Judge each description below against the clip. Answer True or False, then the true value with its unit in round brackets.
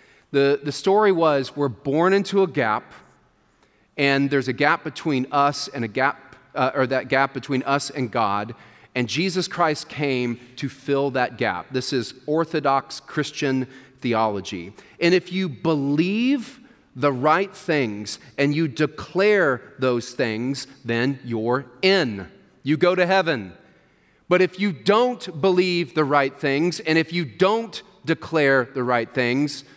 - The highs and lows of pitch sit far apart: False (4.6 semitones)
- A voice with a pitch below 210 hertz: True (140 Hz)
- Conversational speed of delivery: True (150 wpm)